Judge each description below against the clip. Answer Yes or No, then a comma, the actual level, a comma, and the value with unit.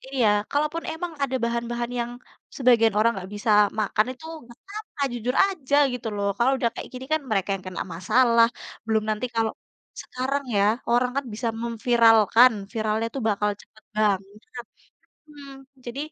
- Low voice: No, high, 235 Hz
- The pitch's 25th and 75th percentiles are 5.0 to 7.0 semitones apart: No, average, 3.3 semitones